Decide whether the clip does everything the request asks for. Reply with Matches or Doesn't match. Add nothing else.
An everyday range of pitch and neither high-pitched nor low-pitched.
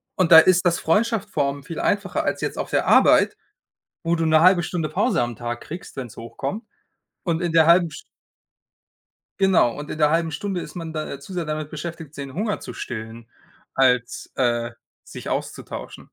Matches